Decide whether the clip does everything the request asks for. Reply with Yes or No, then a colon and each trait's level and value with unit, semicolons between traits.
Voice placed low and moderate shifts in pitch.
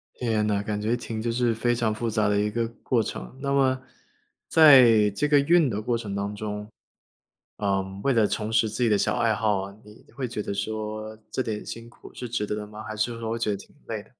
No: low, 110 Hz; narrow, 2.2 semitones